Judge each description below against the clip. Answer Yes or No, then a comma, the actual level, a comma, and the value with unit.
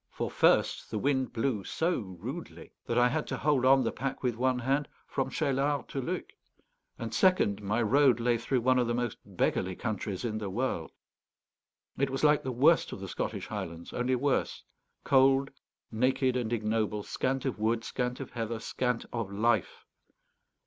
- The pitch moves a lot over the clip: No, average, 3.4 semitones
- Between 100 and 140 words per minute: No, average, 175 wpm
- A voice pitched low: Yes, low, 125 Hz